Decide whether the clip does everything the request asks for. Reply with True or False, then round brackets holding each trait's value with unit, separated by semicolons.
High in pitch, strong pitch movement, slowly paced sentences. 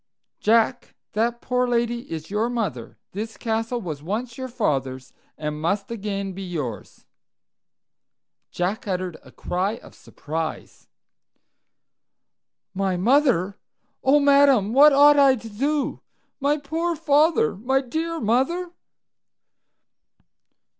True (230 Hz; 6.7 semitones; 115 wpm)